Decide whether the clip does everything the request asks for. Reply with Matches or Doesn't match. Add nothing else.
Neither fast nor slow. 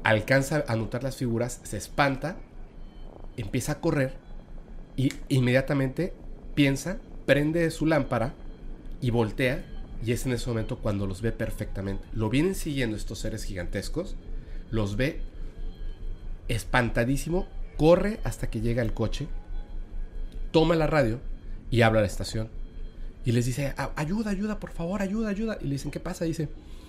Matches